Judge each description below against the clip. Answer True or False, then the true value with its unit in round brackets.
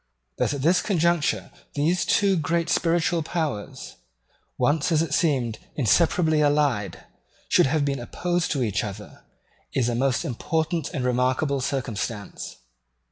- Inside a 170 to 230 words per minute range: False (135 wpm)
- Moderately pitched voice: True (145 Hz)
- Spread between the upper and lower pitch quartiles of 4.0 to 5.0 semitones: True (4.6 semitones)